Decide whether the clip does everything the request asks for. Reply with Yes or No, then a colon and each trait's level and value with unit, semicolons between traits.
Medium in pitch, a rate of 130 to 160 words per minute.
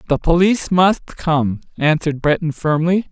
Yes: medium, 160 Hz; slow, 135 wpm